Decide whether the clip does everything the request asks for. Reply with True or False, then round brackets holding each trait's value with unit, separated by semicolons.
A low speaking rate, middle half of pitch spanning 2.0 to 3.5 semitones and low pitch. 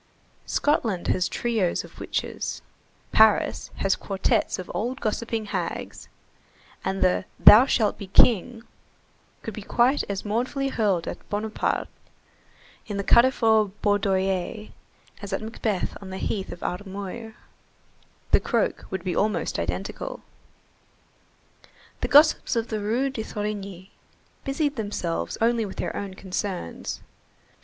False (125 wpm; 3.1 semitones; 210 Hz)